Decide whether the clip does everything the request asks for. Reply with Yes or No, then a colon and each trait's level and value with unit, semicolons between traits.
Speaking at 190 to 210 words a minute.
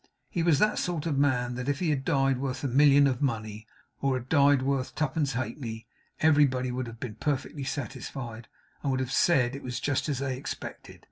Yes: fast, 205 wpm